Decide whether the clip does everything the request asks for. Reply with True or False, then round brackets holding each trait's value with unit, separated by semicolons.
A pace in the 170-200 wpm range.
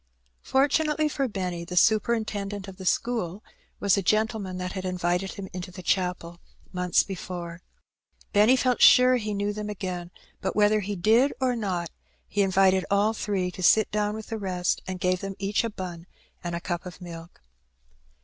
True (180 wpm)